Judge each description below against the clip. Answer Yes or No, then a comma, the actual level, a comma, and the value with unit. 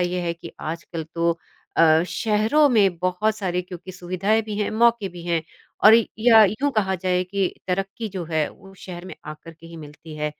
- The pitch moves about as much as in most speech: Yes, average, 3.9 semitones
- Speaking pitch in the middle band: Yes, medium, 180 Hz